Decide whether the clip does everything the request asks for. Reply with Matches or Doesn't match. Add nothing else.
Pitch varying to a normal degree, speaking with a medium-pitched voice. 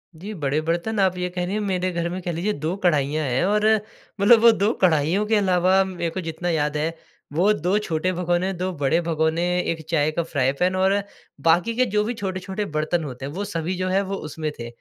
Matches